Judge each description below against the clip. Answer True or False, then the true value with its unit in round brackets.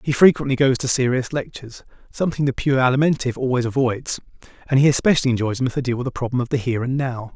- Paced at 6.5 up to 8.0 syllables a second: True (7.2 syllables/s)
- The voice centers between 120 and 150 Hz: True (130 Hz)